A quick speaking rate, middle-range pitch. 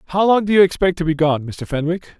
Yes: fast, 275 wpm; medium, 170 Hz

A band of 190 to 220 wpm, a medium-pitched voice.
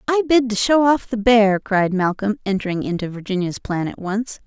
No: average, 200 wpm; high, 215 Hz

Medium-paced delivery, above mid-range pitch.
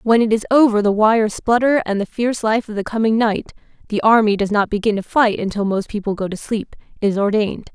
No: fast, 215 wpm; high, 215 Hz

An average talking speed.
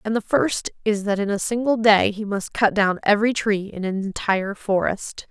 No: fast, 215 wpm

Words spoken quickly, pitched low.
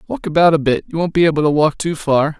No: fast, 300 wpm; medium, 160 Hz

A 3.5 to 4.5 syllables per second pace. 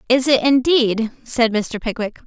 Yes: 4.3 syllables/s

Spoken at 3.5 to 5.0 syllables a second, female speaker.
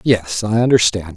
No: 4.6 syllables/s; male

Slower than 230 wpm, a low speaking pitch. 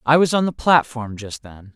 No: fast, 240 wpm; low, 130 Hz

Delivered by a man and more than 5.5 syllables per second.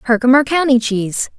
No: female; 6.0 syllables/s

